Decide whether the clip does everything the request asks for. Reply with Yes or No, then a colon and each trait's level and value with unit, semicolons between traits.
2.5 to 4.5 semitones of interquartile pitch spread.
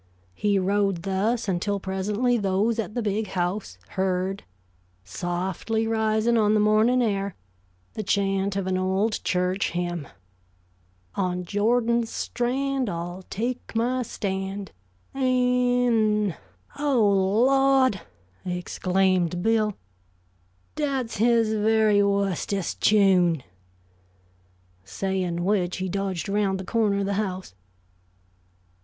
Yes: average, 3.1 semitones